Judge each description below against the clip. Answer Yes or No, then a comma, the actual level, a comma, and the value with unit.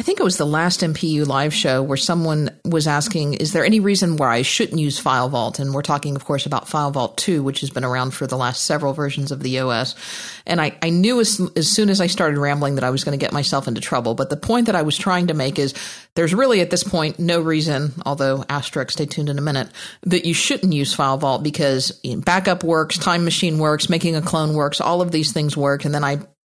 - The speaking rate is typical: No, fast, 250 wpm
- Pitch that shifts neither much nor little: Yes, average, 3.7 semitones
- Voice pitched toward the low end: No, medium, 150 Hz